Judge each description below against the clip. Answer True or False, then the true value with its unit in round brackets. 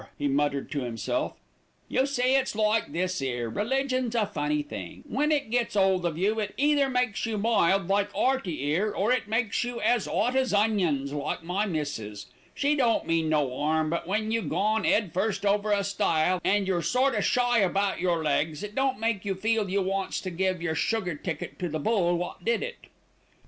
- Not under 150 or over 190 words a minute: False (200 wpm)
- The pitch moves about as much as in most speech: False (5.7 semitones)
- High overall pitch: True (200 Hz)